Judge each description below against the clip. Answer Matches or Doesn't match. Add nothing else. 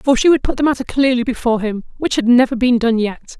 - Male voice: Doesn't match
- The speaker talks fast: Matches